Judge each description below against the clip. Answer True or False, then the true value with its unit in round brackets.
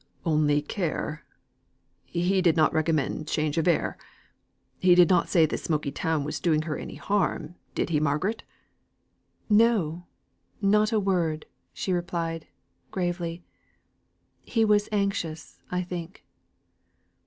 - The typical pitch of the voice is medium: True (170 Hz)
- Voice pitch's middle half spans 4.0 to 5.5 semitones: False (3.4 semitones)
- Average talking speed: False (125 wpm)